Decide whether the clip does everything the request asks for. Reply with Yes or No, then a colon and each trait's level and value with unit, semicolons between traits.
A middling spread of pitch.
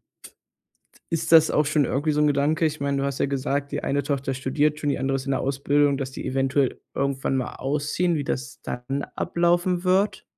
No: narrow, 2.1 semitones